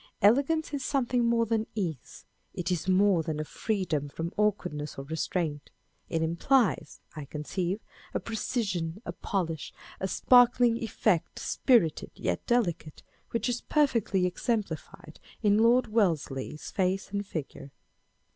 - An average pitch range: No, wide, 6.2 semitones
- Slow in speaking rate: Yes, slow, 130 wpm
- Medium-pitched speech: No, high, 195 Hz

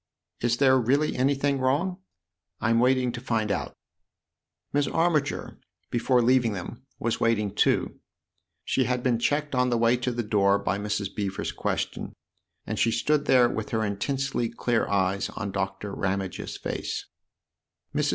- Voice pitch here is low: Yes, low, 120 Hz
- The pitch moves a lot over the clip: No, average, 4.3 semitones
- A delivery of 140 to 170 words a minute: Yes, average, 160 wpm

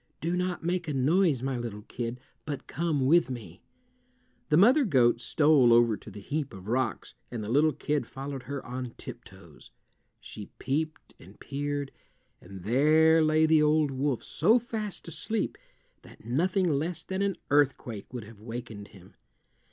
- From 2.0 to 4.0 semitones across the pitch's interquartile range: No, average, 5.2 semitones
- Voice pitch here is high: No, medium, 140 Hz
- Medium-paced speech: Yes, average, 160 wpm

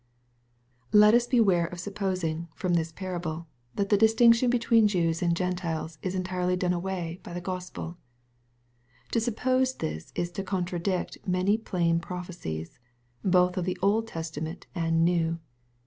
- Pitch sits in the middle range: Yes, medium, 180 Hz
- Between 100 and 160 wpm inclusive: Yes, average, 145 wpm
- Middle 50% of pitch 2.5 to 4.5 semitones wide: Yes, average, 3.0 semitones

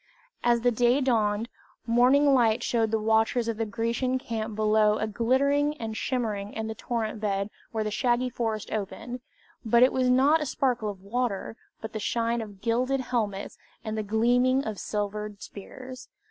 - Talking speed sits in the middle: Yes, average, 170 wpm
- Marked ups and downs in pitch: No, narrow, 2.6 semitones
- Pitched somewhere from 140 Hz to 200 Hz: No, high, 230 Hz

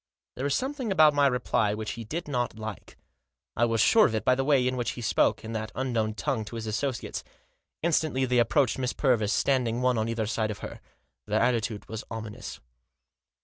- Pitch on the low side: Yes, low, 120 Hz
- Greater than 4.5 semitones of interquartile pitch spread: No, average, 3.4 semitones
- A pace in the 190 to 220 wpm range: Yes, fast, 205 wpm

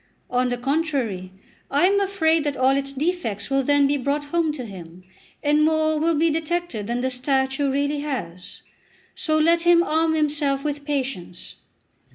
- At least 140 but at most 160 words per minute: No, average, 170 wpm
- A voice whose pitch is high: Yes, very high, 285 Hz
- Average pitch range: Yes, average, 3.4 semitones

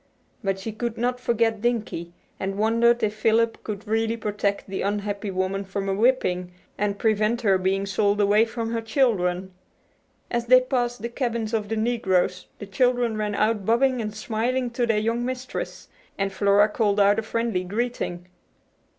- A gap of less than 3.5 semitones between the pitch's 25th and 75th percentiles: Yes, average, 2.9 semitones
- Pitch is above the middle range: Yes, high, 215 Hz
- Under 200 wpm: Yes, average, 170 wpm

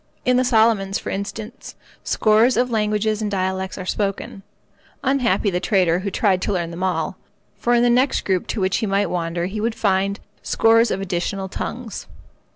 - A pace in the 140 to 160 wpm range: No, average, 180 wpm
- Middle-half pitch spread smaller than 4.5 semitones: Yes, average, 3.1 semitones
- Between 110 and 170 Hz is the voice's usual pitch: No, high, 200 Hz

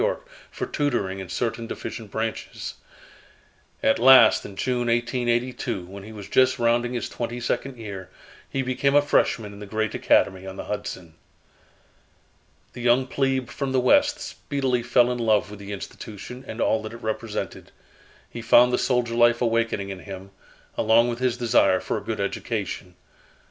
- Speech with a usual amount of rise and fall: Yes, average, 3.1 semitones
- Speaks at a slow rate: No, average, 170 wpm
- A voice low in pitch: Yes, low, 120 Hz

